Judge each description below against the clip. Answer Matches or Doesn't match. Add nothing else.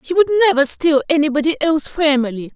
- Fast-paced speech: Doesn't match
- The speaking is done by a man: Doesn't match